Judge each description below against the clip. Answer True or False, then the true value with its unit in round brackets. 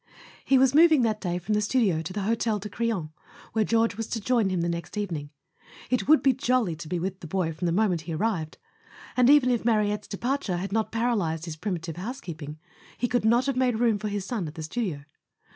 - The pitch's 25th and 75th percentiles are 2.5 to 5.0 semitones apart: False (5.6 semitones)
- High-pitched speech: True (210 Hz)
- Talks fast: True (235 wpm)